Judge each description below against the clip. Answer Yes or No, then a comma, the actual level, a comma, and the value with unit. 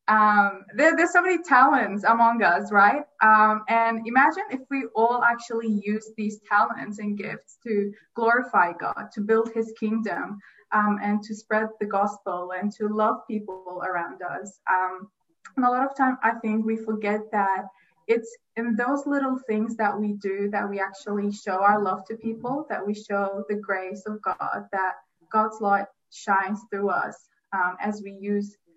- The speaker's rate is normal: Yes, average, 175 wpm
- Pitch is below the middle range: No, high, 210 Hz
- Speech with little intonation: Yes, narrow, 2.3 semitones